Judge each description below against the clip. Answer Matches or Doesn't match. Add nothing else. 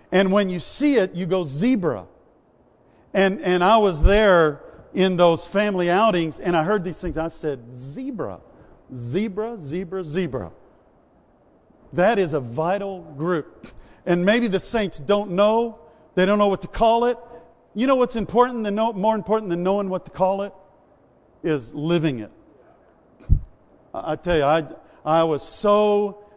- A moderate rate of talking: Matches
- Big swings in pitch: Doesn't match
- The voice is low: Doesn't match